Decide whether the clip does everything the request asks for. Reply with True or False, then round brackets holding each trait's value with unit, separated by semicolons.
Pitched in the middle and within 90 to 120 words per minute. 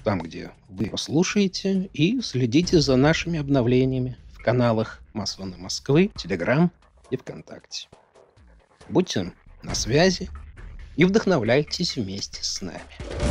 False (130 Hz; 110 wpm)